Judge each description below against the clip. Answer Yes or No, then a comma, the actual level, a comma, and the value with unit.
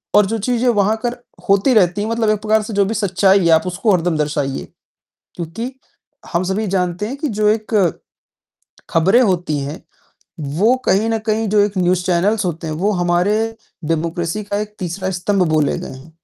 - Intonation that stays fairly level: No, average, 3.7 semitones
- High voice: Yes, high, 195 Hz